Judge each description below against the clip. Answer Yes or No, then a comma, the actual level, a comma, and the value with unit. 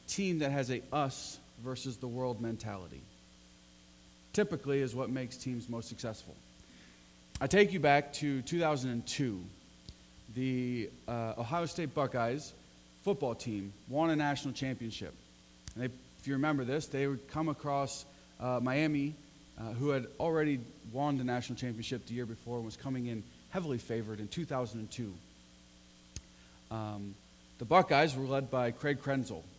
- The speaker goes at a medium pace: Yes, average, 145 wpm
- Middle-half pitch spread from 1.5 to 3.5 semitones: No, average, 5.1 semitones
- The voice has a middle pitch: No, low, 125 Hz